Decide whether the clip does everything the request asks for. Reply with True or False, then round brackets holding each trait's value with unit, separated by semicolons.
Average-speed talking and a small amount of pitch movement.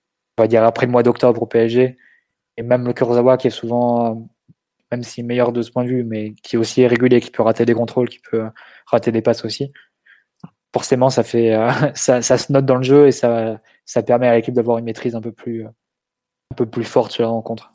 False (235 wpm; 1.4 semitones)